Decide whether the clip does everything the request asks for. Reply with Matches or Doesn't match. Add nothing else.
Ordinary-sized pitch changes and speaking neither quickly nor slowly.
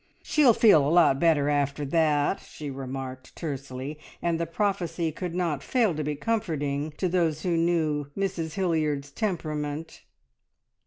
Matches